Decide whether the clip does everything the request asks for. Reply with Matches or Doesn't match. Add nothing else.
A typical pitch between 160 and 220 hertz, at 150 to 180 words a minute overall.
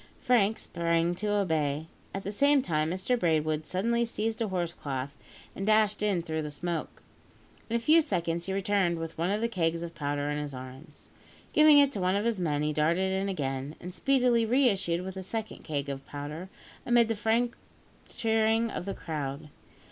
Doesn't match